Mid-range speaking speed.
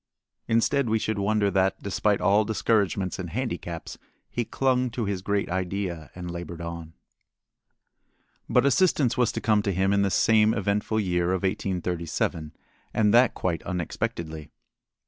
Yes: average, 145 wpm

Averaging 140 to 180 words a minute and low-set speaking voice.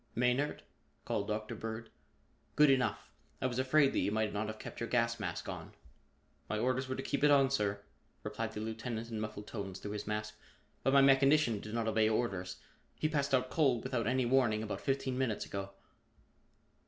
No: average, 190 wpm; low, 115 Hz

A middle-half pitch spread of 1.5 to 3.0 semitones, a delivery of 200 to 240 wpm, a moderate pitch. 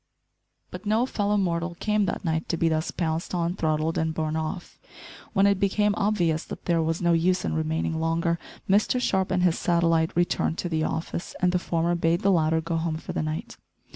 Yes: narrow, 2.5 semitones; fast, 205 wpm; medium, 170 Hz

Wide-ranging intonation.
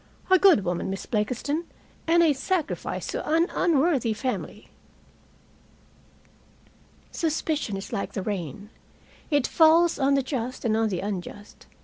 Yes: wide, 7.6 semitones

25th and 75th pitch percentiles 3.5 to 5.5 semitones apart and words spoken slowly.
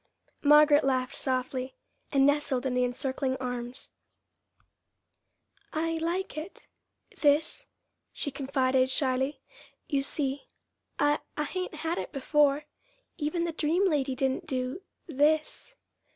No: average, 3.0 semitones; slow, 115 wpm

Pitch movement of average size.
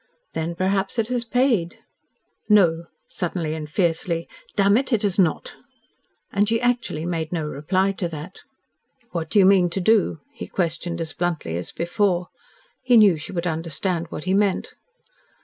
Yes: average, 3.5 semitones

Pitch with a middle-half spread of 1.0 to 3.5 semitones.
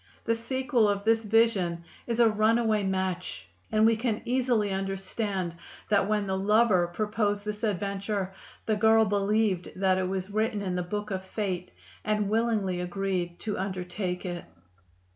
Yes: narrow, 2.6 semitones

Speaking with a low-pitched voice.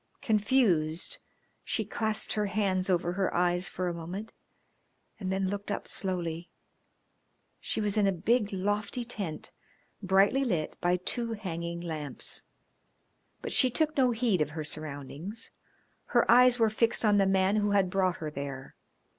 No: high, 190 Hz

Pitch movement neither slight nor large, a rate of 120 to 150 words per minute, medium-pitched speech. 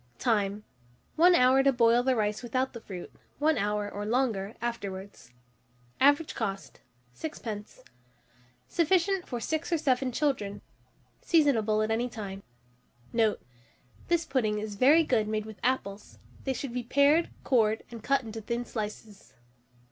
No: average, 4.4 semitones; average, 140 wpm; high, 235 Hz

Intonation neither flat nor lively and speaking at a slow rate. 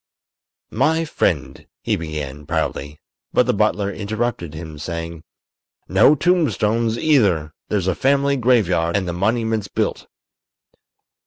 No: wide, 6.4 semitones; slow, 115 wpm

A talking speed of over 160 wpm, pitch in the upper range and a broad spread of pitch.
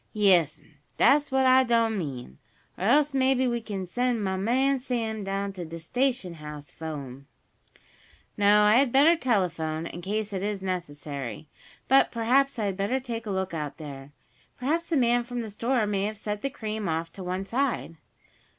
Yes: average, 185 wpm; high, 210 Hz; wide, 6.3 semitones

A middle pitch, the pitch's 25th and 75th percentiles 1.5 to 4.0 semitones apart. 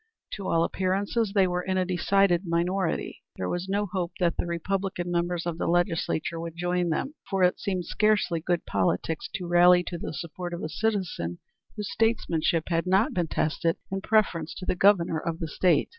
Yes: medium, 175 Hz; narrow, 2.4 semitones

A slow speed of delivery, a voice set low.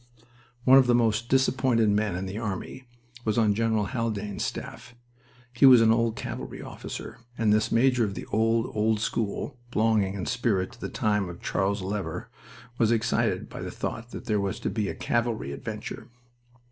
No: average, 180 wpm; low, 110 Hz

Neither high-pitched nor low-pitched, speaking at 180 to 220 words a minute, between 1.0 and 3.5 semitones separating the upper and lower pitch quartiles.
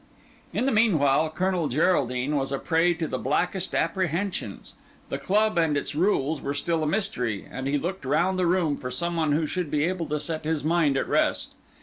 No: medium, 160 Hz; fast, 205 wpm; average, 4.1 semitones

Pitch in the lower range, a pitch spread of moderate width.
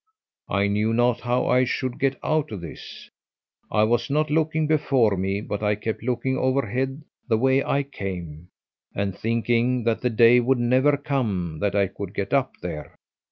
Yes: low, 120 Hz; average, 4.6 semitones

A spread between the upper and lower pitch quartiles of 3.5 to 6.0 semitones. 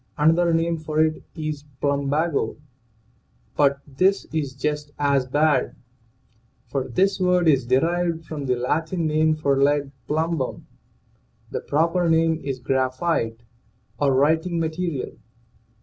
No: average, 3.0 semitones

